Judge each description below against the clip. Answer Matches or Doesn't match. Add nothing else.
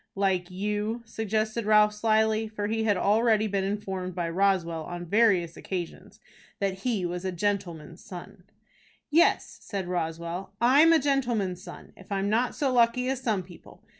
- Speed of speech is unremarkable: Matches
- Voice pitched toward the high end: Matches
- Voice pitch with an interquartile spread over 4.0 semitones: Doesn't match